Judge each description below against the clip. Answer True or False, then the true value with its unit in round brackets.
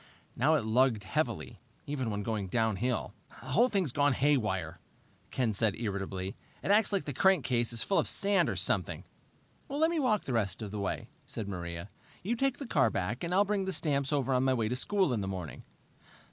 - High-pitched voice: False (130 Hz)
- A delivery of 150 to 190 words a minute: False (200 wpm)